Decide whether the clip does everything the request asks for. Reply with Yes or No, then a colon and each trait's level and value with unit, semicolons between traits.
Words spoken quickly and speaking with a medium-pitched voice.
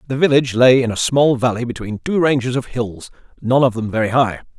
No: fast, 220 wpm; low, 125 Hz